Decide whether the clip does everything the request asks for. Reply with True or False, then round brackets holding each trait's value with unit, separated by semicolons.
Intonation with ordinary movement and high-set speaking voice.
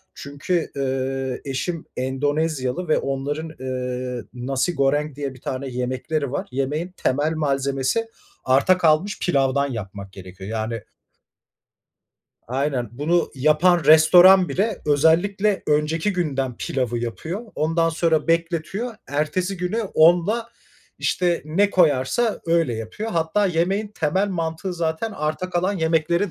False (4.9 semitones; 155 Hz)